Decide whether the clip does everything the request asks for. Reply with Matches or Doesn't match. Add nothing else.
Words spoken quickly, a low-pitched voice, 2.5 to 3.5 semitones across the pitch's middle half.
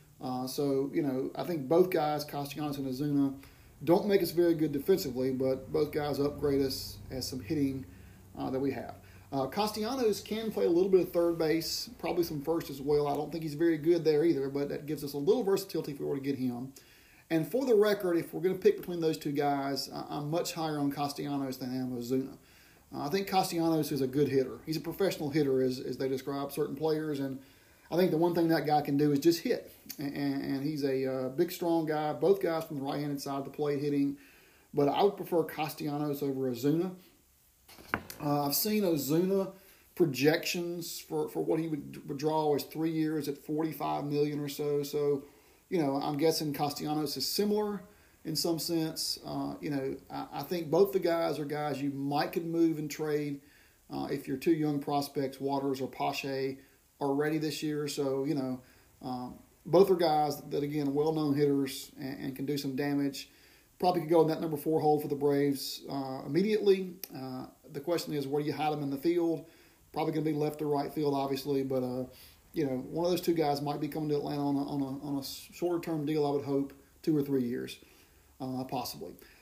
Doesn't match